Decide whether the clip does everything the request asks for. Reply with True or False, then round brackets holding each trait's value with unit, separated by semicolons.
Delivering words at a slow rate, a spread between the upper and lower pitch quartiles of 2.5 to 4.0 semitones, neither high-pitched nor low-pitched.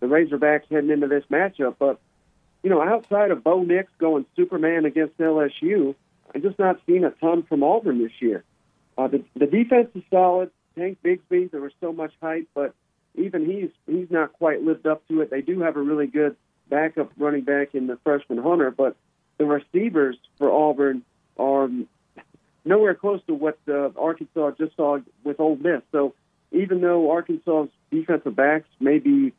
False (180 wpm; 3.4 semitones; 155 Hz)